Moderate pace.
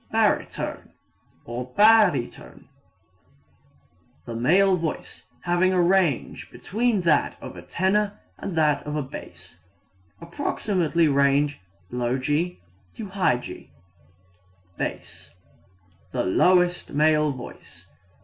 No: slow, 90 wpm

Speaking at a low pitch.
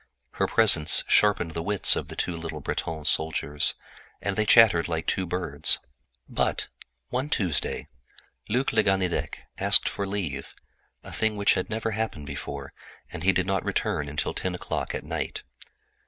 Yes: very low, 90 Hz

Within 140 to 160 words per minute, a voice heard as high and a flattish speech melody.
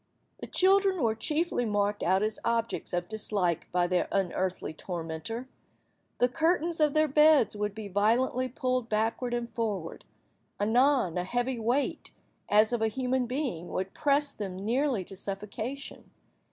No: average, 150 wpm; high, 230 Hz; average, 4.8 semitones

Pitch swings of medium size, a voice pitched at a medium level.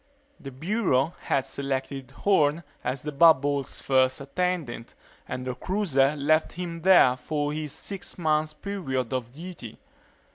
Yes: average, 4.2 semitones; medium, 145 Hz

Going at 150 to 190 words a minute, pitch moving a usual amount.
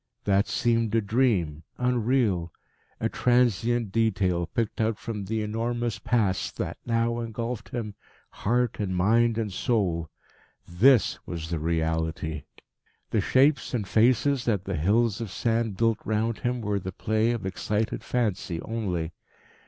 No: average, 140 wpm; average, 3.8 semitones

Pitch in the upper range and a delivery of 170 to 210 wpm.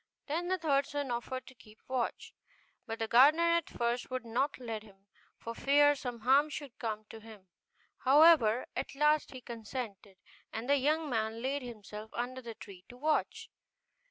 Yes: very high, 250 Hz; average, 175 wpm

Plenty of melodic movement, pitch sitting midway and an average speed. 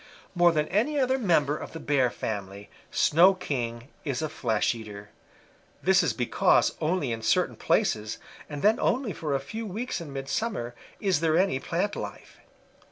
Yes: wide, 7.8 semitones; medium, 155 Hz; average, 165 wpm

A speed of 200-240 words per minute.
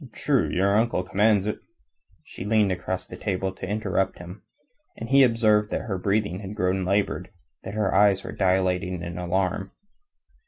No: average, 165 wpm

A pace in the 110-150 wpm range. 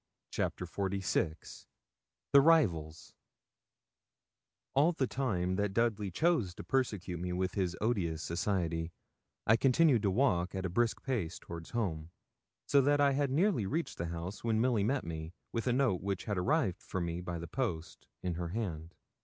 No: average, 165 wpm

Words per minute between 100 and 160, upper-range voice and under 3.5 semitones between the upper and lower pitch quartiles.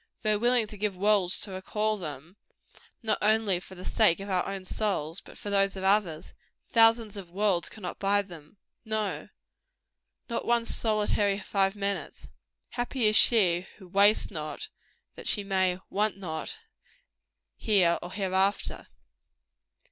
Yes: average, 145 wpm; high, 200 Hz; narrow, 2.5 semitones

